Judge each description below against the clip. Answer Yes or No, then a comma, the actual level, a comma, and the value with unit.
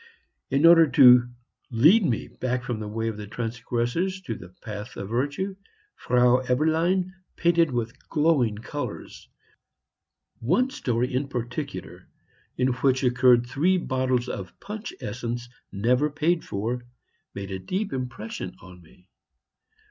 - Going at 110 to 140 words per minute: Yes, slow, 135 wpm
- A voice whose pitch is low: Yes, low, 125 Hz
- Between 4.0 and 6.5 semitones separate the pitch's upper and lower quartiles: Yes, average, 5.1 semitones